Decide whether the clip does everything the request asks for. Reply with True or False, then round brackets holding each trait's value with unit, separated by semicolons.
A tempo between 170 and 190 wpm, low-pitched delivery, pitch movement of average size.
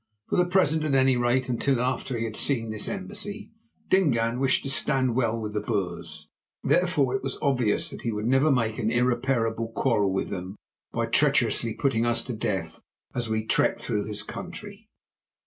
True (180 wpm; 120 Hz; 3.7 semitones)